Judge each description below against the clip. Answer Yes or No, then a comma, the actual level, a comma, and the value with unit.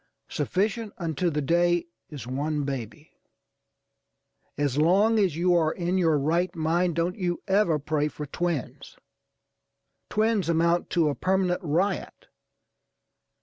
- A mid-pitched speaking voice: Yes, medium, 170 Hz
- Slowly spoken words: Yes, slow, 125 wpm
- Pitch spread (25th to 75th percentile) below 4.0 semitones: Yes, average, 3.3 semitones